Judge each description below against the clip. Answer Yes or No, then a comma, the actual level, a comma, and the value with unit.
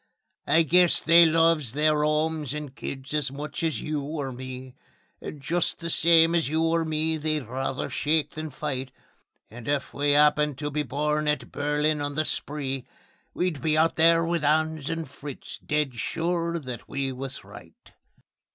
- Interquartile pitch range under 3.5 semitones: Yes, narrow, 2.5 semitones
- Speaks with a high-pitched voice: No, medium, 150 Hz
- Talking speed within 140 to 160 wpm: No, average, 170 wpm